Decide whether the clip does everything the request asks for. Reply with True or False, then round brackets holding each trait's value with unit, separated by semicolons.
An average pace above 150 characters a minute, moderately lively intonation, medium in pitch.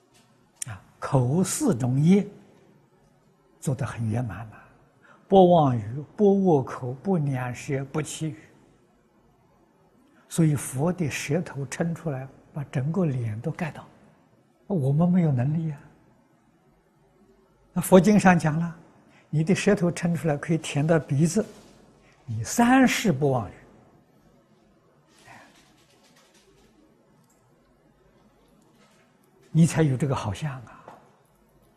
False (145 characters per minute; 4.6 semitones; 155 Hz)